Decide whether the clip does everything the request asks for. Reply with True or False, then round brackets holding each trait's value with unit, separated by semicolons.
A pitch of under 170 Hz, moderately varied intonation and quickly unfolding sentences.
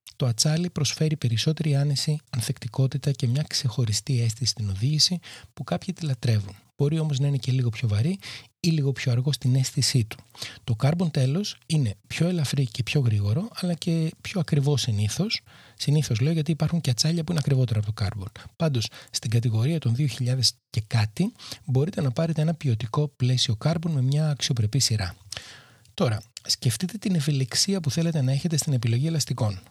True (135 Hz; 4.6 semitones; 175 wpm)